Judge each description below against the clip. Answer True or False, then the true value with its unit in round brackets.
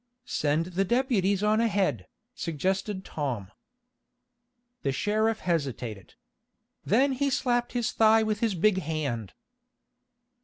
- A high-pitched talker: True (195 Hz)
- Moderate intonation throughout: False (6.9 semitones)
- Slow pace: True (110 wpm)